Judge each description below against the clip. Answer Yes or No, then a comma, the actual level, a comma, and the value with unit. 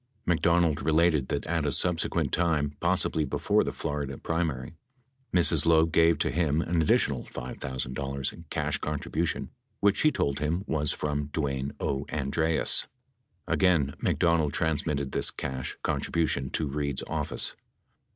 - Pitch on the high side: No, very low, 75 Hz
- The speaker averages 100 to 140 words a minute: Yes, slow, 135 wpm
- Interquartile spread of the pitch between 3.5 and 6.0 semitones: No, average, 2.9 semitones